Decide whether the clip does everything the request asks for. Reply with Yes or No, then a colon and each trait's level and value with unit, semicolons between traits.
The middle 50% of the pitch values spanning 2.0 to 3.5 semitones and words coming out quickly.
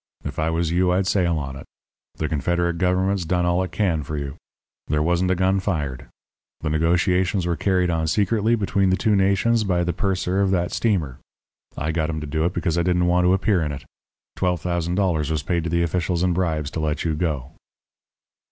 Yes: average, 2.8 semitones; fast, 215 wpm